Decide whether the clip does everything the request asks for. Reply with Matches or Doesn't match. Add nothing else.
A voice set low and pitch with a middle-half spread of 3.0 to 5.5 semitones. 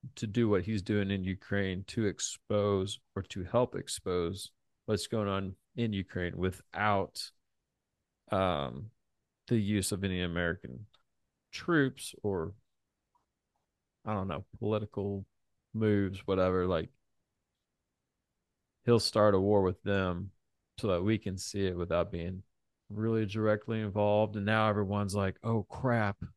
Doesn't match